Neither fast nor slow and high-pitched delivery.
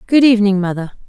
Yes: average, 165 wpm; high, 210 Hz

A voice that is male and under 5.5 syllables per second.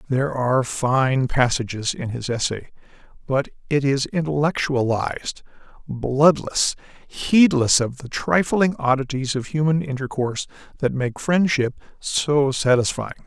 Yes: male; 4.3 syllables/s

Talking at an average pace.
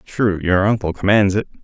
Yes: average, 185 wpm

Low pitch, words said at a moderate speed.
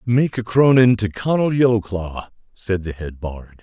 Yes: low, 105 Hz; average, 165 wpm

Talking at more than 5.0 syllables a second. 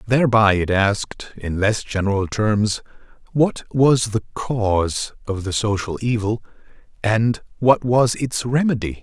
No: 4.1 syllables/s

